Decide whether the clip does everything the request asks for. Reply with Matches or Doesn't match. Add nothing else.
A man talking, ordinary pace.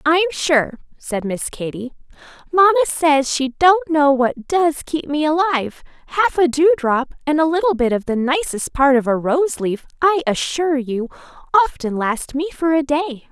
Doesn't match